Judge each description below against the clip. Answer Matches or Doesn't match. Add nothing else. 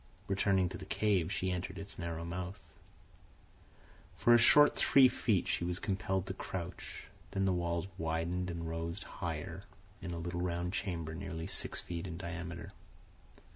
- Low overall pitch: Matches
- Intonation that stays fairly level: Matches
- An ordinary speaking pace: Matches